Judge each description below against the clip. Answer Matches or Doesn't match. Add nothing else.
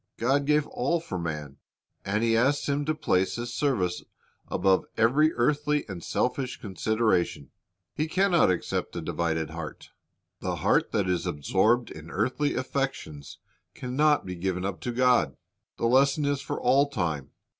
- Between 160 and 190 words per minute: Matches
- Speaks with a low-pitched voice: Matches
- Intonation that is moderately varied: Doesn't match